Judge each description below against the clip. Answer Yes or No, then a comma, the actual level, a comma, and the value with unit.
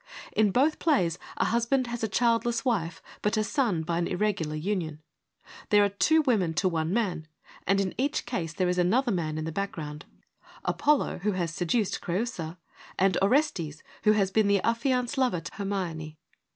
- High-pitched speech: Yes, high, 195 Hz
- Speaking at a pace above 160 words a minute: Yes, average, 180 wpm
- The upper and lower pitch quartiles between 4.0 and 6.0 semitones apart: Yes, wide, 5.6 semitones